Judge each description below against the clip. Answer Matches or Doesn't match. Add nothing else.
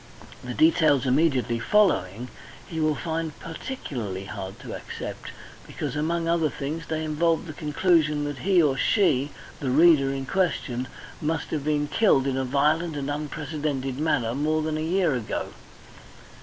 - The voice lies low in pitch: Doesn't match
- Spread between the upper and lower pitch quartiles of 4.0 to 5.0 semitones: Doesn't match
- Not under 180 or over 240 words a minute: Doesn't match